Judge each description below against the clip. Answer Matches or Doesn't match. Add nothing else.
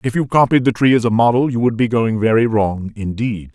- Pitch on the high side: Doesn't match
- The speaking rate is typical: Doesn't match